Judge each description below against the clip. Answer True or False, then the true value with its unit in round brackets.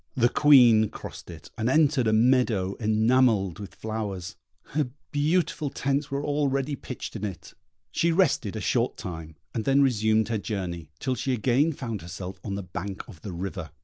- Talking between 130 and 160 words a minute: False (175 wpm)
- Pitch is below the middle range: True (110 Hz)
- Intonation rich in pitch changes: True (5.7 semitones)